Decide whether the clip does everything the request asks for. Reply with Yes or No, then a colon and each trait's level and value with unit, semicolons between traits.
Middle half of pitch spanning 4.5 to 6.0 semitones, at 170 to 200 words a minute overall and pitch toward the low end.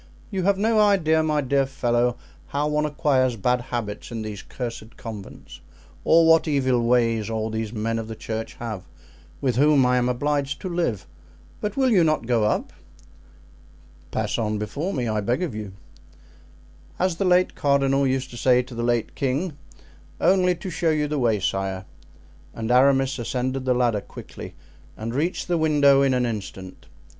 Yes: average, 4.8 semitones; average, 175 wpm; low, 130 Hz